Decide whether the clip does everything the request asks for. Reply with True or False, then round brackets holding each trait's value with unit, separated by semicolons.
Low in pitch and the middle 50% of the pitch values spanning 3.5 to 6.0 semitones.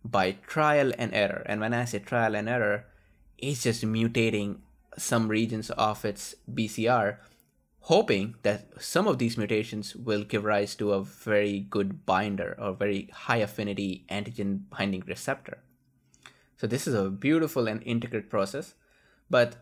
False (110 Hz; 2.8 semitones)